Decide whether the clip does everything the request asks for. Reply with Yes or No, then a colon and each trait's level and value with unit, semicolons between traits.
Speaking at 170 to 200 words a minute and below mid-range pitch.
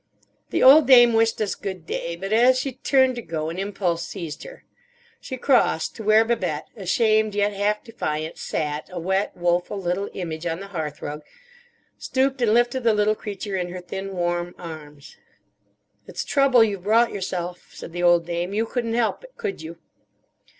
No: average, 180 wpm; high, 195 Hz